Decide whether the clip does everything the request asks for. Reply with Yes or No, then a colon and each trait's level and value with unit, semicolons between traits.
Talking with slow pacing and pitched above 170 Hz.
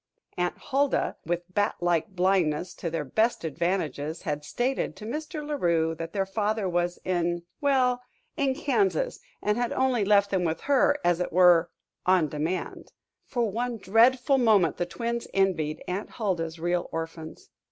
No: average, 160 wpm; high, 190 Hz